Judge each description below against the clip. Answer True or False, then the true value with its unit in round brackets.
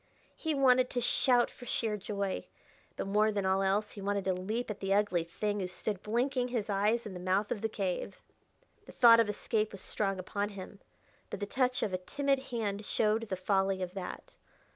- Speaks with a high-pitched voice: True (205 Hz)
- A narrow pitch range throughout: False (3.0 semitones)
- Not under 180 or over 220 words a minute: True (205 wpm)